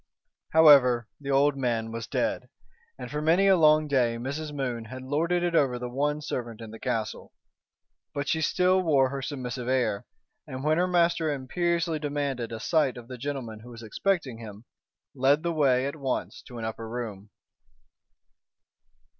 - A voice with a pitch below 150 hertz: Yes, low, 135 Hz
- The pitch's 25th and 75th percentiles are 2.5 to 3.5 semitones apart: No, average, 4.3 semitones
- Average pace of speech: Yes, average, 170 wpm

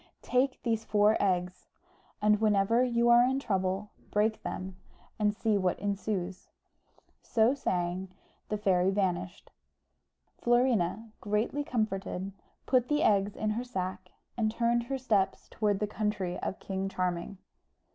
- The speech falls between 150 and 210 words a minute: No, slow, 135 wpm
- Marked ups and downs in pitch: No, average, 3.6 semitones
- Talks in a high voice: Yes, high, 210 Hz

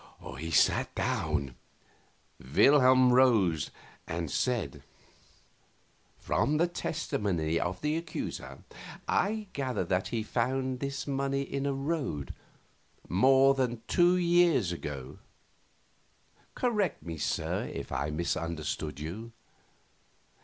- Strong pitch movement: Yes, wide, 9.0 semitones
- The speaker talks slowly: Yes, slow, 105 wpm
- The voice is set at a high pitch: No, low, 125 Hz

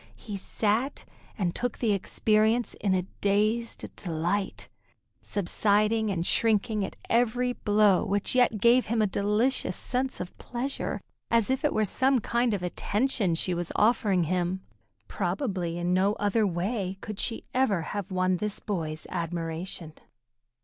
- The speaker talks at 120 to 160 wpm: Yes, average, 145 wpm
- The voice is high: Yes, high, 205 Hz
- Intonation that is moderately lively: Yes, average, 4.0 semitones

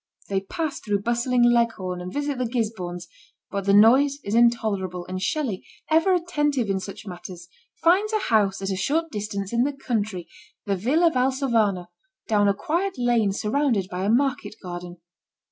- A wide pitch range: Yes, wide, 5.9 semitones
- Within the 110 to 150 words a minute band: No, average, 165 wpm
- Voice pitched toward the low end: No, high, 220 Hz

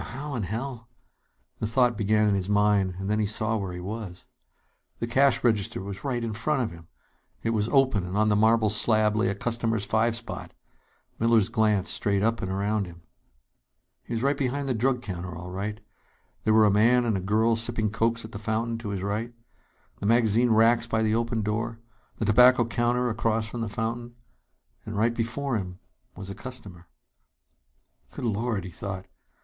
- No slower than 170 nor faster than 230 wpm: Yes, average, 195 wpm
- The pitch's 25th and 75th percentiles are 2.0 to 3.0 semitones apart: Yes, narrow, 2.4 semitones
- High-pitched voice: No, low, 110 Hz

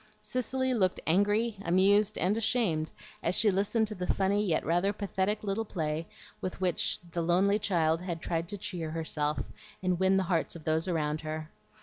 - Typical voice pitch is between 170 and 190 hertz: Yes, medium, 185 Hz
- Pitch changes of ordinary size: Yes, average, 3.8 semitones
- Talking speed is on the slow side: No, average, 180 wpm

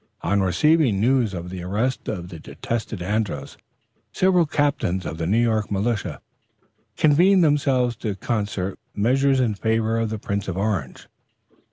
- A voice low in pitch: Yes, low, 110 Hz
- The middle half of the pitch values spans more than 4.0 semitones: Yes, average, 5.2 semitones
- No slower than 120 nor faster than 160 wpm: Yes, average, 150 wpm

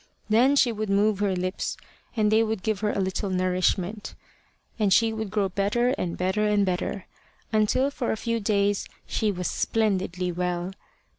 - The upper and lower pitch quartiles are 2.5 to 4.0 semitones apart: Yes, average, 2.9 semitones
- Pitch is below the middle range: No, high, 205 Hz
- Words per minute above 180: No, average, 170 wpm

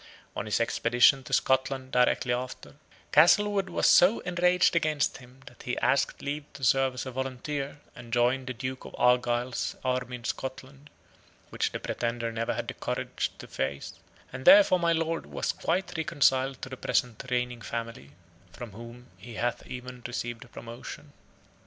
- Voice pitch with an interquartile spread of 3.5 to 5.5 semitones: No, average, 2.9 semitones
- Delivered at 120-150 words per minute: No, average, 165 wpm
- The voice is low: Yes, low, 130 Hz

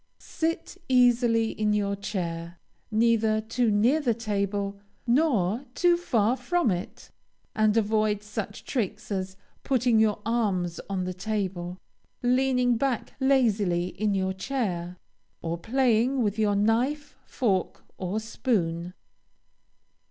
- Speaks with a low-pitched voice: No, high, 215 Hz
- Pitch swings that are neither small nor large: Yes, average, 4.0 semitones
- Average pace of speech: No, slow, 120 wpm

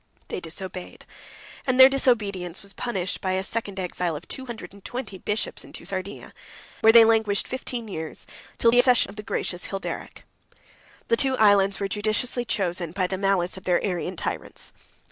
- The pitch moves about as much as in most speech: Yes, average, 3.8 semitones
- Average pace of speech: Yes, average, 180 wpm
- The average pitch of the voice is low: No, high, 200 Hz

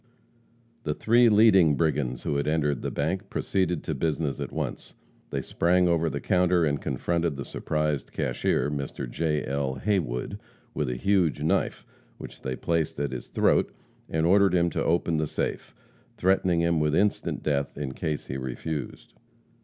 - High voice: No, very low, 80 Hz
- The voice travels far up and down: No, average, 3.4 semitones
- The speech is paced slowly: No, average, 165 wpm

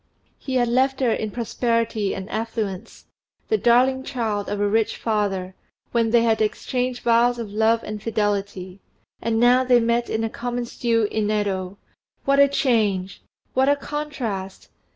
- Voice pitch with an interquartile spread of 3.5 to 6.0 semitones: No, average, 3.0 semitones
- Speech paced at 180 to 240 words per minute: No, average, 160 wpm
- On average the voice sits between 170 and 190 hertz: No, high, 230 Hz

